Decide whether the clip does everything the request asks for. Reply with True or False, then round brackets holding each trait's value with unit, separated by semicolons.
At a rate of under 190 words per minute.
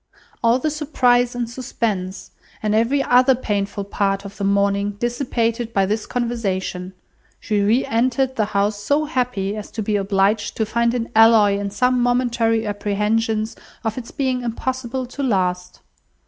True (155 wpm)